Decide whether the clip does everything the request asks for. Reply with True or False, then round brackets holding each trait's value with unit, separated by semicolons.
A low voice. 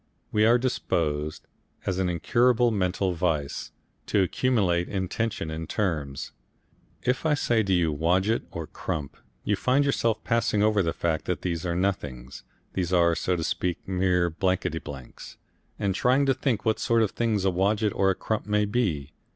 True (95 Hz)